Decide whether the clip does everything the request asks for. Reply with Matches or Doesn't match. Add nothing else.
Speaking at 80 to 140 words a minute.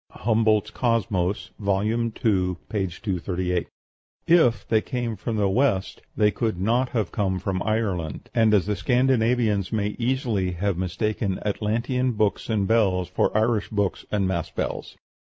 Matches